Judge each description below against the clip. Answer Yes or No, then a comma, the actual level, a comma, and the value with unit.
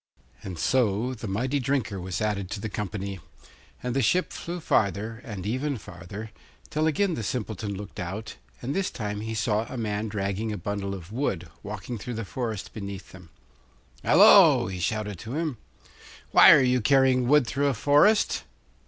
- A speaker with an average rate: Yes, average, 175 wpm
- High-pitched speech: No, low, 110 Hz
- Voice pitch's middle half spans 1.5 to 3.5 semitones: No, average, 4.4 semitones